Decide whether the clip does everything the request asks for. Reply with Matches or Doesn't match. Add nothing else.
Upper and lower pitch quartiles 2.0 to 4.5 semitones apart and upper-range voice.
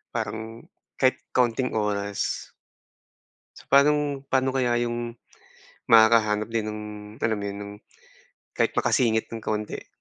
Doesn't match